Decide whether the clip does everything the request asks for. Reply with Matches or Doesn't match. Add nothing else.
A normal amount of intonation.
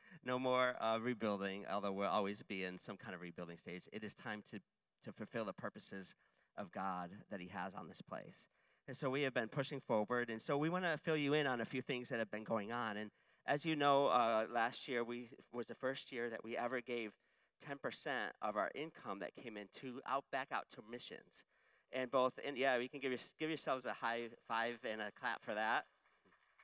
Matches